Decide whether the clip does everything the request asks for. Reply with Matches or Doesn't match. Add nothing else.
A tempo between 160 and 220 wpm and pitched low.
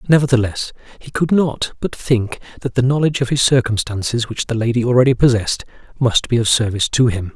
Matches